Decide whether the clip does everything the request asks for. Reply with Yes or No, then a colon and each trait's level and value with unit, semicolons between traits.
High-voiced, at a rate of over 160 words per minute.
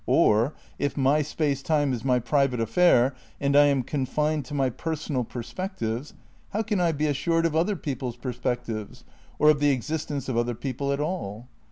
No: medium, 140 Hz; average, 185 wpm